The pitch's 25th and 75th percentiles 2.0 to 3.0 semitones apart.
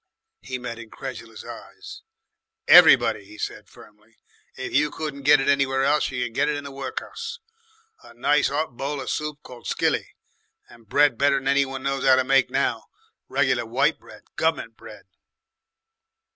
Yes: narrow, 2.6 semitones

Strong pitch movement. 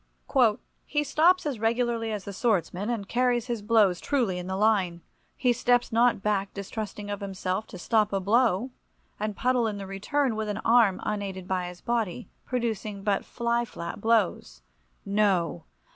No: average, 3.5 semitones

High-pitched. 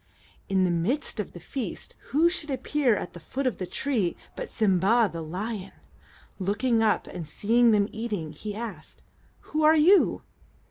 Yes: high, 220 Hz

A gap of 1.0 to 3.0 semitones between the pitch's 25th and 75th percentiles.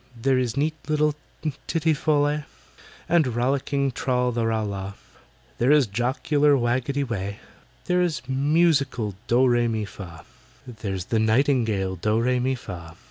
No: average, 4.5 semitones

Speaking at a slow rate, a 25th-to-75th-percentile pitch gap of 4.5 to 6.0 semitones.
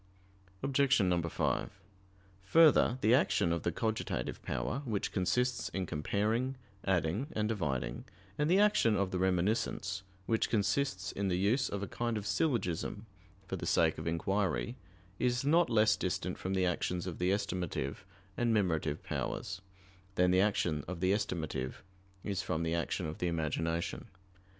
No: average, 155 wpm; average, 5.0 semitones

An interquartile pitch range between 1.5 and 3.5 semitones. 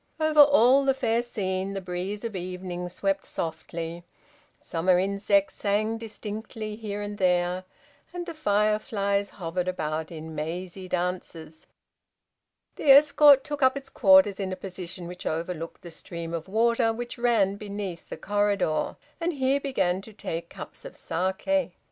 No: average, 4.5 semitones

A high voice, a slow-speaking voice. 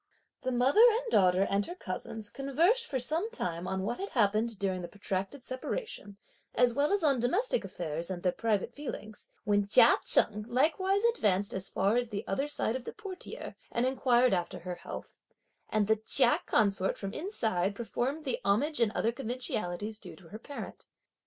No: high, 230 Hz; average, 180 wpm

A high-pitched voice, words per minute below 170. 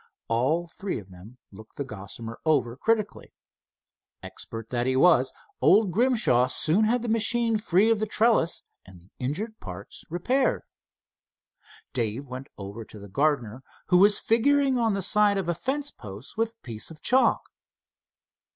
No: medium, 165 Hz; average, 160 wpm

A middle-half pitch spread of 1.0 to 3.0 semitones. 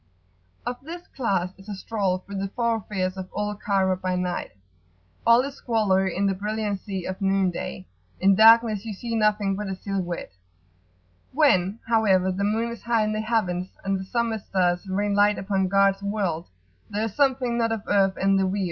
Yes: average, 2.7 semitones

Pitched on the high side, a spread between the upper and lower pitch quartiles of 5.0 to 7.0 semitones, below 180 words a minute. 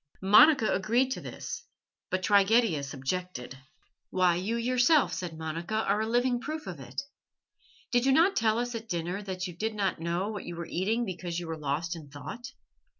No: high, 195 Hz; wide, 5.5 semitones; average, 185 wpm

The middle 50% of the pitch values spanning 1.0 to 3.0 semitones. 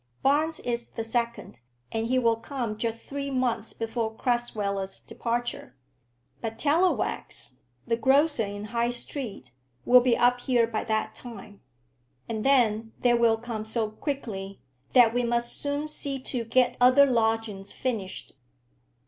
Yes: narrow, 2.4 semitones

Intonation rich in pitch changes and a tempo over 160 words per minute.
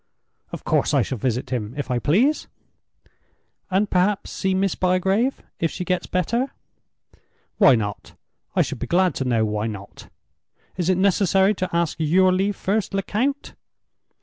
No: wide, 6.5 semitones; average, 150 wpm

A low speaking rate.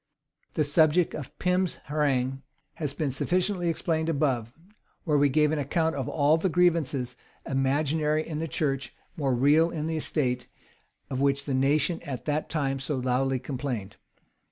No: average, 155 wpm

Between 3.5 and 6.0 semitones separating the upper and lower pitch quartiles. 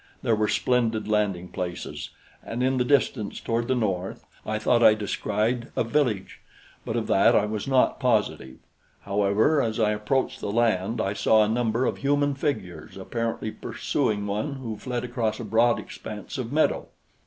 No: average, 3.0 semitones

